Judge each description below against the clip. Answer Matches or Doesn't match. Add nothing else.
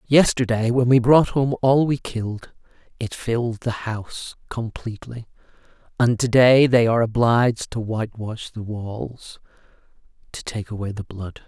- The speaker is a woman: Doesn't match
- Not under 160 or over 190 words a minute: Doesn't match